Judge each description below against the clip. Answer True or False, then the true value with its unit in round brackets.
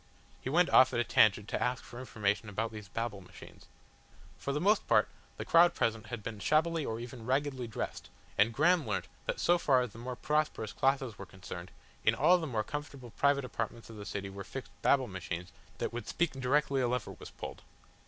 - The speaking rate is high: True (210 wpm)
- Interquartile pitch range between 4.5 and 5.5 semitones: True (4.8 semitones)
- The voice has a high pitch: False (125 Hz)